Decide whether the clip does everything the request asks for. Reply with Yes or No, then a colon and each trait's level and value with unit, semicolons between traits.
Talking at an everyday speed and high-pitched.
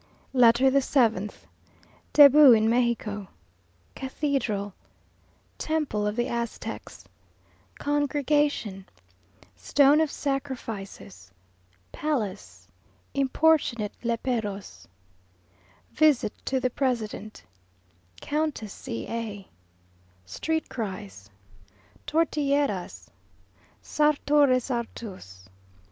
No: slow, 70 wpm; high, 240 Hz